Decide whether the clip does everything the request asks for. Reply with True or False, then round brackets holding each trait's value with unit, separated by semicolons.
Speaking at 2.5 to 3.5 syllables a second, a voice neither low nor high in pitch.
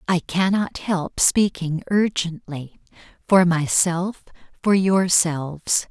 True (3.4 syllables/s; 175 Hz)